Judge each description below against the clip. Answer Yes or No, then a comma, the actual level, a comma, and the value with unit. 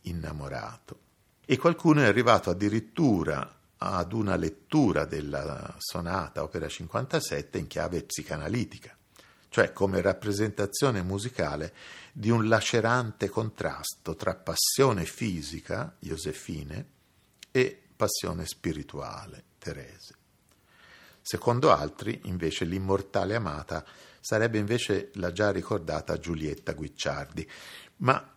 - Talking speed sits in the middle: No, slow, 95 wpm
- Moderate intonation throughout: Yes, average, 4.3 semitones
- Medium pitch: No, low, 100 Hz